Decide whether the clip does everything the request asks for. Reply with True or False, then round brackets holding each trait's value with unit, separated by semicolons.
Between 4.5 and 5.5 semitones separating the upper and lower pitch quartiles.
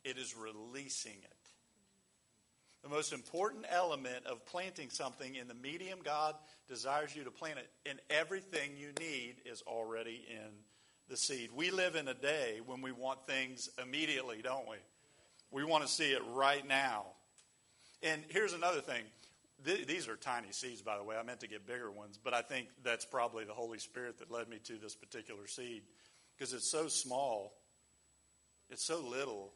True (5.1 semitones)